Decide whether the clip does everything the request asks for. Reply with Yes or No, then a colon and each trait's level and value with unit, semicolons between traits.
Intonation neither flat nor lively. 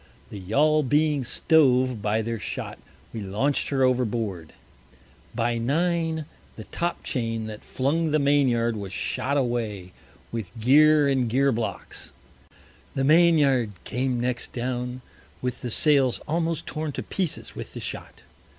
Yes: average, 4.4 semitones